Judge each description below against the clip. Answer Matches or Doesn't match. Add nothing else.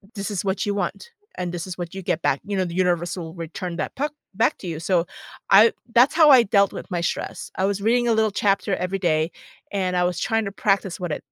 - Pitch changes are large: Doesn't match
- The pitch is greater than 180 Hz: Matches